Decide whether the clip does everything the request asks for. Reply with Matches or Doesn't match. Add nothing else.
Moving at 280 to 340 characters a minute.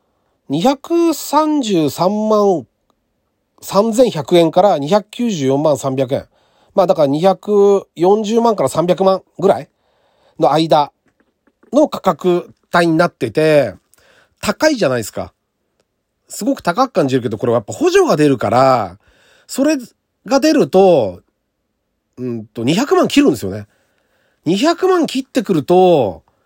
Doesn't match